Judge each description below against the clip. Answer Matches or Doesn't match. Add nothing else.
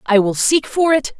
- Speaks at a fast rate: Matches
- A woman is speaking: Matches